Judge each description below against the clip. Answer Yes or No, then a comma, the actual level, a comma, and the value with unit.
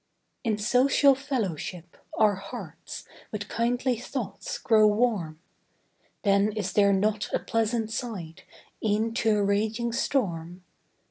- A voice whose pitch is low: No, high, 215 Hz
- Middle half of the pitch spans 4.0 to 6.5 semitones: No, average, 2.9 semitones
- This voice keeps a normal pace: No, slow, 120 wpm